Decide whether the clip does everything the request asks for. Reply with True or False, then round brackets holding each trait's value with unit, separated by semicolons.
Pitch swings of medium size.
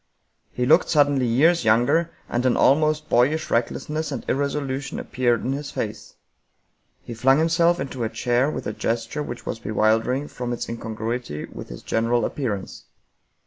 True (4.1 semitones)